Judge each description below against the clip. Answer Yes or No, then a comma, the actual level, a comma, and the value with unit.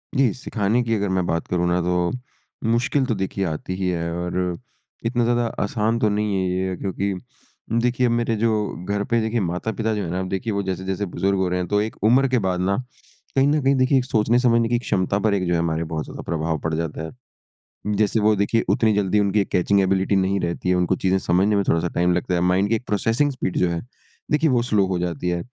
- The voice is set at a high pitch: No, low, 100 Hz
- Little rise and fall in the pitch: No, average, 4.1 semitones